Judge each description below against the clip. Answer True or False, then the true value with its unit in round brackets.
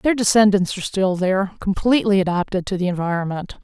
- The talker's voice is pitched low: False (195 Hz)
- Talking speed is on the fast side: False (165 wpm)